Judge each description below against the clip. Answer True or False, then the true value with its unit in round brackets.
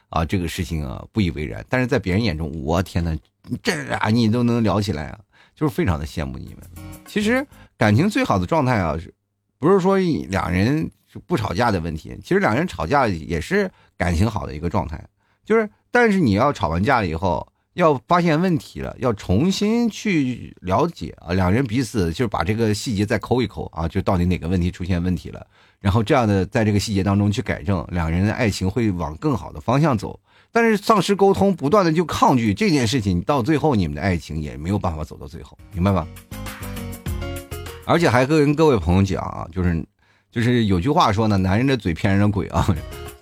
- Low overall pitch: True (100 Hz)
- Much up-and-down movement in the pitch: True (6.1 semitones)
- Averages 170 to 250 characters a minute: False (310 characters per minute)